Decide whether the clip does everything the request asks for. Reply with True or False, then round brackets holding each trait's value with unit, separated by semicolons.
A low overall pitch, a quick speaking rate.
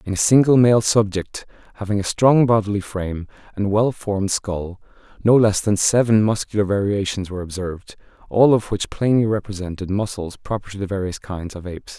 False (100 Hz; 170 wpm)